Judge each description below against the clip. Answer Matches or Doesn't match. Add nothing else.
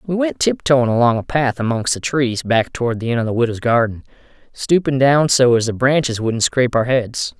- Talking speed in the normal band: Doesn't match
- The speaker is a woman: Doesn't match